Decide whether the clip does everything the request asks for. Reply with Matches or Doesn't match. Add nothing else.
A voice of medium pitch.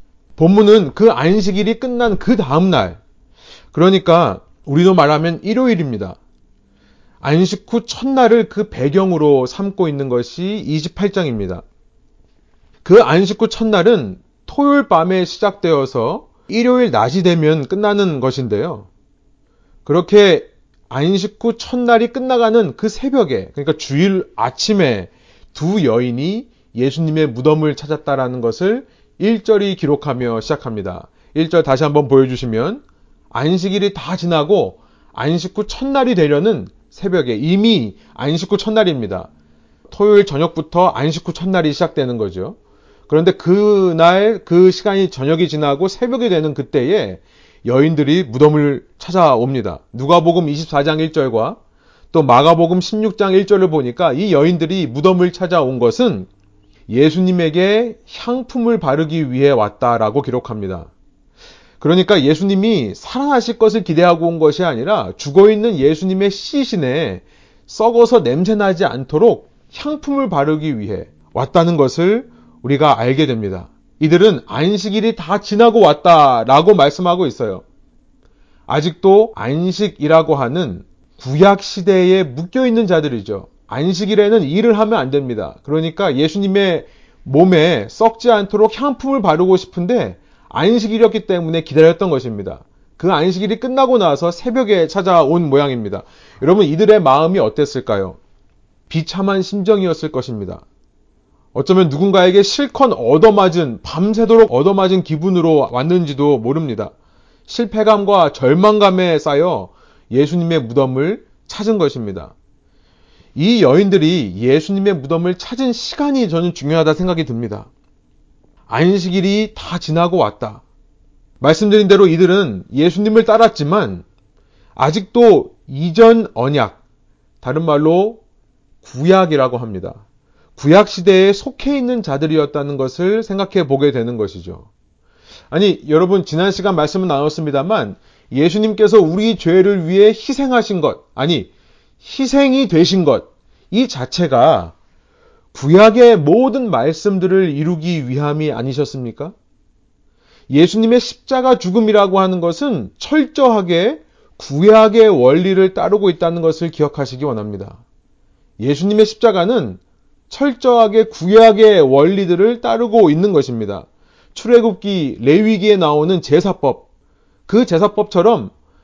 Matches